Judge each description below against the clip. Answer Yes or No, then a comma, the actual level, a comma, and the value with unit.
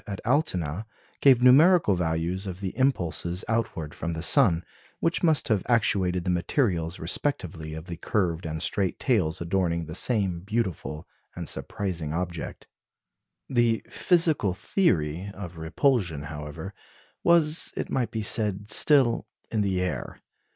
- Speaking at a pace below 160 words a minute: Yes, average, 140 wpm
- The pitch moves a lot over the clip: Yes, wide, 5.9 semitones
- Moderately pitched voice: No, very low, 95 Hz